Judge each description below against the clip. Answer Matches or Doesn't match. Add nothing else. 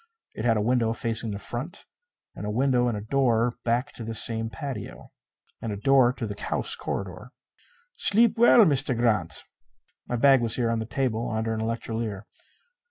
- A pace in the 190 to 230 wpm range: Doesn't match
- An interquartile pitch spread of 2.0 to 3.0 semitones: Matches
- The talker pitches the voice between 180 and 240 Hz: Doesn't match